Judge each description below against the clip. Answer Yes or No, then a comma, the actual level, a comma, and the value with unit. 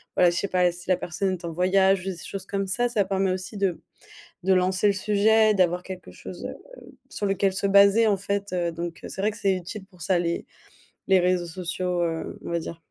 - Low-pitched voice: No, medium, 185 Hz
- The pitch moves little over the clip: Yes, narrow, 2.0 semitones